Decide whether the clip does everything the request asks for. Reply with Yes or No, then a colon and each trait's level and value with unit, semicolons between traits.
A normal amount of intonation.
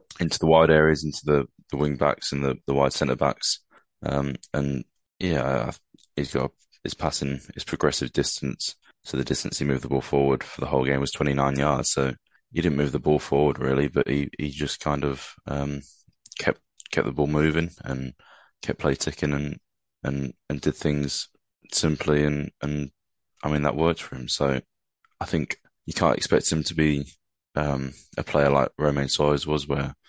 No: narrow, 1.4 semitones